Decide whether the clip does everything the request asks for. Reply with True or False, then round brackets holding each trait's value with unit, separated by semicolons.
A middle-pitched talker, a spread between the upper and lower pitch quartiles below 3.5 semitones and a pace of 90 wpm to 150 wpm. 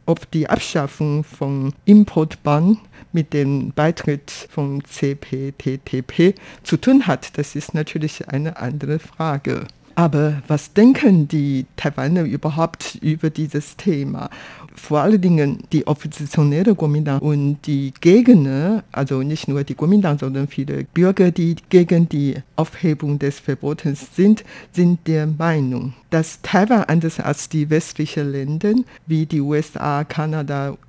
True (150 Hz; 2.9 semitones; 130 wpm)